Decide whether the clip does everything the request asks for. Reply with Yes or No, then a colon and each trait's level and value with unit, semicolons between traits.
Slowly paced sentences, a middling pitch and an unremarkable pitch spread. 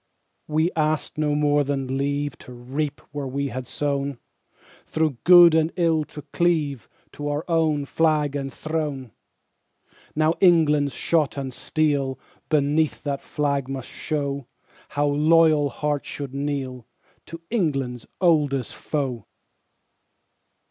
No: slow, 125 wpm; medium, 145 Hz; narrow, 2.2 semitones